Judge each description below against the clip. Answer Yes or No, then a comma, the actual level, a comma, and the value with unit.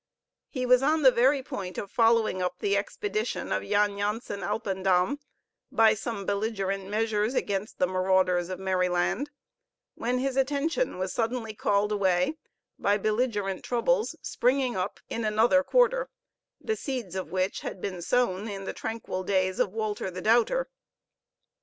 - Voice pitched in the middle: No, high, 210 Hz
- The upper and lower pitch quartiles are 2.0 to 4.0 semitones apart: No, average, 4.7 semitones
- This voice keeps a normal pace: Yes, average, 150 wpm